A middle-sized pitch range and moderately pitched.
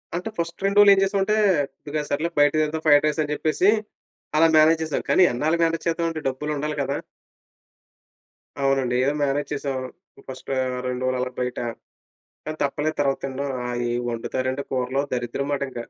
Yes: average, 3.4 semitones; medium, 145 Hz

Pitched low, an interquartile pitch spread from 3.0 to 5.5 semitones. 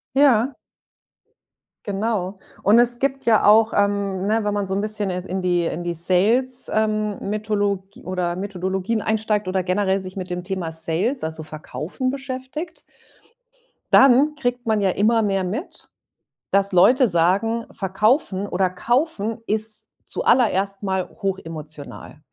No: high, 200 Hz; average, 3.5 semitones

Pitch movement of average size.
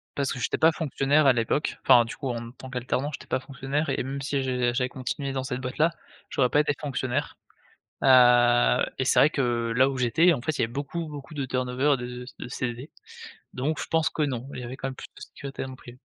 No: narrow, 2.3 semitones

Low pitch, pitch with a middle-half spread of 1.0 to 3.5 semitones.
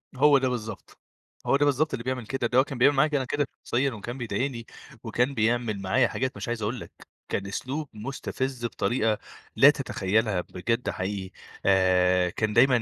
No: low, 120 Hz; average, 4.0 semitones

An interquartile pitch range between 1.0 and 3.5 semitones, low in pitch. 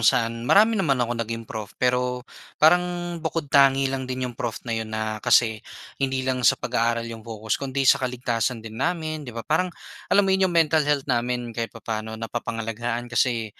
Yes: average, 3.1 semitones; low, 125 Hz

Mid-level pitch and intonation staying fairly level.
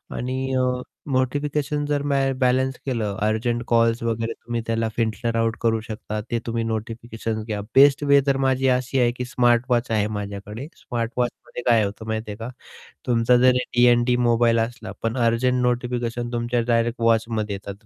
No: low, 120 Hz; narrow, 1.8 semitones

